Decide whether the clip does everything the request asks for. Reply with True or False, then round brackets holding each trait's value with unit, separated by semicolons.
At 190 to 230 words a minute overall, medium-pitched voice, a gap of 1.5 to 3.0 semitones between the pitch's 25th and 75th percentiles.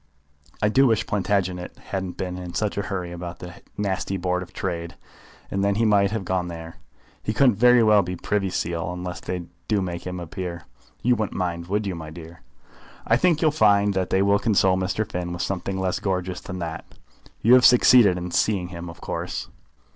False (205 wpm; 95 Hz; 2.7 semitones)